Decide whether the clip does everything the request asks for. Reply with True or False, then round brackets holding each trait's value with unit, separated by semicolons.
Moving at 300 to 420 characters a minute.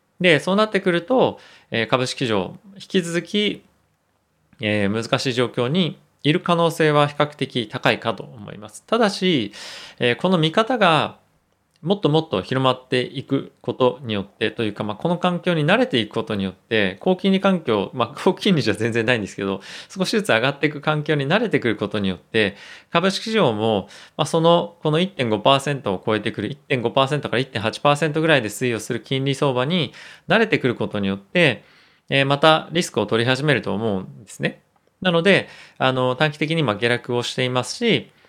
True (335 characters per minute)